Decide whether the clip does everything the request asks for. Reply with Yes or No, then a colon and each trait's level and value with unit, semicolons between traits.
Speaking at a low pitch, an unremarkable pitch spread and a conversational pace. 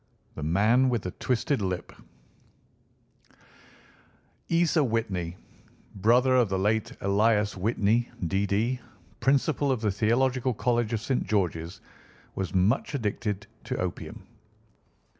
No: low, 110 Hz; average, 4.5 semitones; slow, 110 wpm